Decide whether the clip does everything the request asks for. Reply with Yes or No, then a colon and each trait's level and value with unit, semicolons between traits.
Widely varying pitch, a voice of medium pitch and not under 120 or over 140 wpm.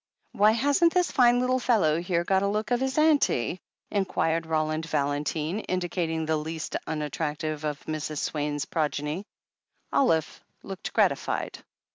Yes: wide, 5.8 semitones; medium, 165 Hz; slow, 135 wpm